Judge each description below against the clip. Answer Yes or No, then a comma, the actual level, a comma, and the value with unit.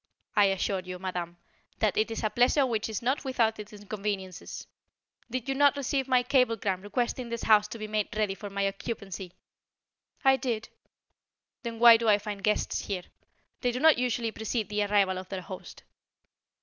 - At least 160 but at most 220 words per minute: Yes, average, 180 wpm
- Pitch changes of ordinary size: Yes, average, 3.5 semitones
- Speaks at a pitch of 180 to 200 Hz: No, high, 215 Hz